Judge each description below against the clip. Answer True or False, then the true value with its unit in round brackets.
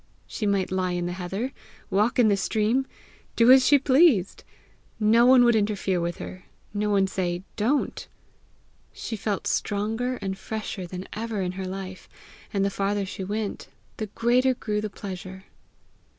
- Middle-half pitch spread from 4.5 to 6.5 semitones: False (3.3 semitones)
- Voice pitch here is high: True (205 Hz)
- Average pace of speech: True (165 wpm)